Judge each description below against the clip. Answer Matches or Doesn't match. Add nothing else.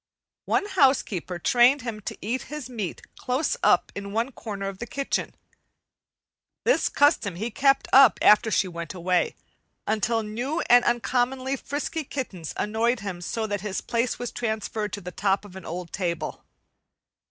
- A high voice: Matches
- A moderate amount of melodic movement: Matches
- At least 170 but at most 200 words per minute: Doesn't match